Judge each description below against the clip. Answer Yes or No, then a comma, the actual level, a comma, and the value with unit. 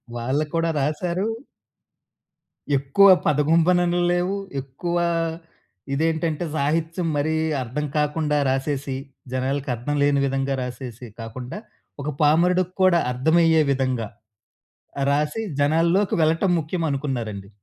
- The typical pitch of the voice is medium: Yes, medium, 150 Hz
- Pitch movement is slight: No, average, 3.8 semitones